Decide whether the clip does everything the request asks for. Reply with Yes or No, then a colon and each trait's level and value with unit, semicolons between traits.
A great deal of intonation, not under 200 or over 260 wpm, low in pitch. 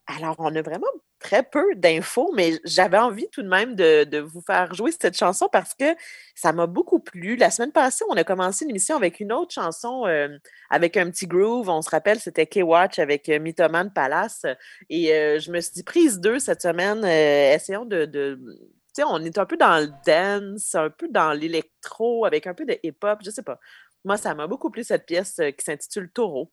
No: wide, 6.4 semitones; fast, 220 wpm; medium, 185 Hz